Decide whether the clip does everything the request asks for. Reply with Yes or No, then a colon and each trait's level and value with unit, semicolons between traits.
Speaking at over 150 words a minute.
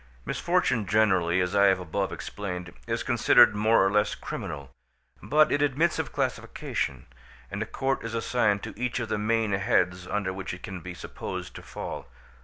Yes: average, 180 wpm